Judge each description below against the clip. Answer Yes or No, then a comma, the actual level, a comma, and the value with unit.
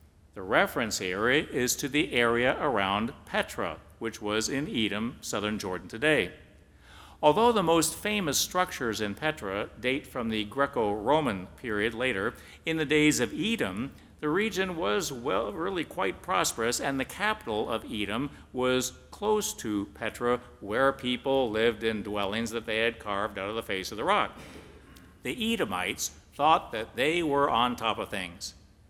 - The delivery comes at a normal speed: Yes, average, 160 wpm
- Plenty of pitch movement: Yes, wide, 5.9 semitones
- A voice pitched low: Yes, low, 120 Hz